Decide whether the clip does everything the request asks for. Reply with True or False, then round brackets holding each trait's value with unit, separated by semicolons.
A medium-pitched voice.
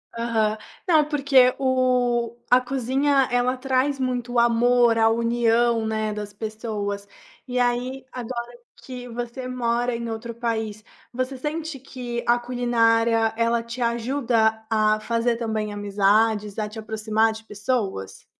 False (235 Hz)